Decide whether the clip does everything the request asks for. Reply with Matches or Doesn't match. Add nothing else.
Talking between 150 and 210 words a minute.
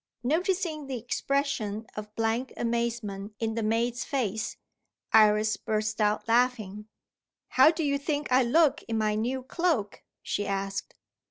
Doesn't match